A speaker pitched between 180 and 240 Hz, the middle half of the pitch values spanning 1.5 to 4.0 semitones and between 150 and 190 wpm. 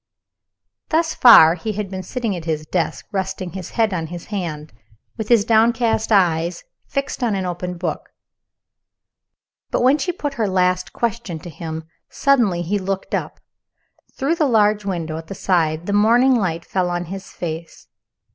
No: high, 190 Hz; average, 4.7 semitones; average, 165 wpm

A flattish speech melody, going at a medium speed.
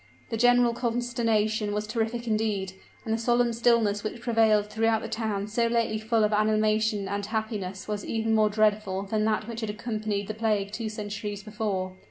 Yes: narrow, 1.6 semitones; average, 180 wpm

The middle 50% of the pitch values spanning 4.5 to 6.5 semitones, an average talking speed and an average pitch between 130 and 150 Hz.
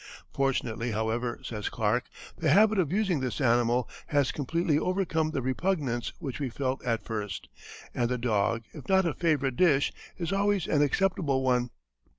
Yes: wide, 5.6 semitones; average, 160 wpm; low, 135 Hz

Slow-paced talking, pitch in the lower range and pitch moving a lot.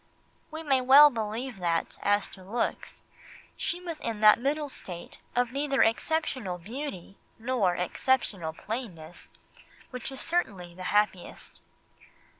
No: slow, 125 wpm; high, 230 Hz; wide, 6.5 semitones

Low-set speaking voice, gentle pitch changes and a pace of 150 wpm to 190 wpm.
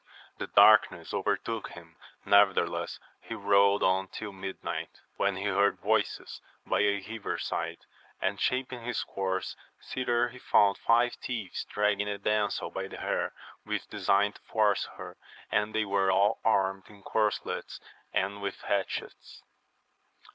No: low, 100 Hz; narrow, 1.9 semitones; average, 140 wpm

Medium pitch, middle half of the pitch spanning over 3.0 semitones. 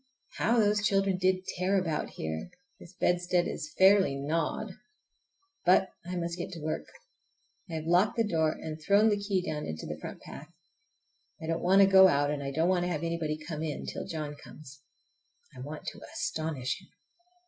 Yes: medium, 170 Hz; average, 3.6 semitones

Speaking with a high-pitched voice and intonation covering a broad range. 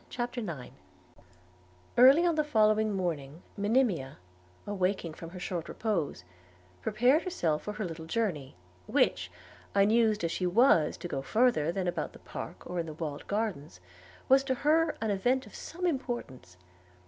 Yes: high, 200 Hz; wide, 6.9 semitones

